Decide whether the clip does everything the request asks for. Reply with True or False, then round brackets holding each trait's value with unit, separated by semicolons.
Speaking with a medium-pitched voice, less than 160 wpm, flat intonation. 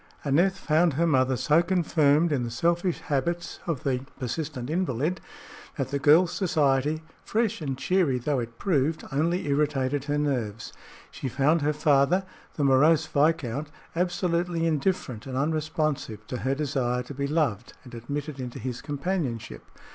False (145 Hz; 150 wpm; 4.0 semitones)